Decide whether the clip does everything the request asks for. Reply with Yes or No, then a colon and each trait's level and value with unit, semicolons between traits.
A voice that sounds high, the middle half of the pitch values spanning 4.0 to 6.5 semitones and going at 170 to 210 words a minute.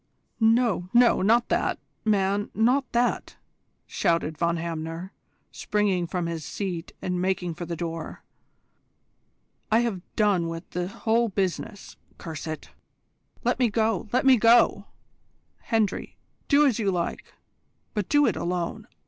No: high, 195 Hz; average, 4.8 semitones; slow, 135 wpm